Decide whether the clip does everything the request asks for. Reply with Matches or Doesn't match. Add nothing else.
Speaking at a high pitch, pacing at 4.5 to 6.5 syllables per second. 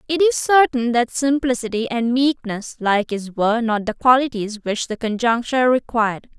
Matches